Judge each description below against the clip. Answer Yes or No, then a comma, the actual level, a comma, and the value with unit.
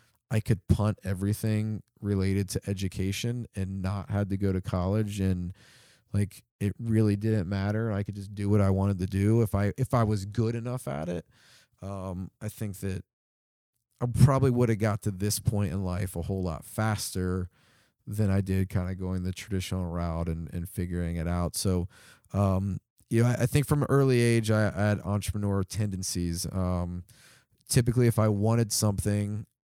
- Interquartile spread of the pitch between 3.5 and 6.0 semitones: No, average, 2.9 semitones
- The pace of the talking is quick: No, average, 185 wpm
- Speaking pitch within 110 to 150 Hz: No, low, 100 Hz